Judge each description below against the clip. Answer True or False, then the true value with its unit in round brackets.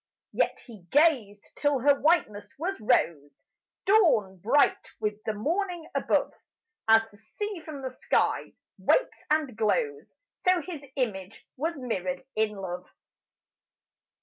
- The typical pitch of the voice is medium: False (250 Hz)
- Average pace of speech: False (125 wpm)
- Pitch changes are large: True (7.7 semitones)